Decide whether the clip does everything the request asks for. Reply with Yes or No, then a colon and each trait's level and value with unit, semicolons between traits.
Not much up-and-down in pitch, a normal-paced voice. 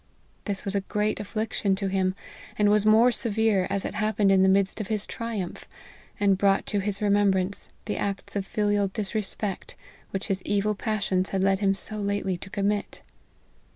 Yes: narrow, 1.5 semitones; average, 185 wpm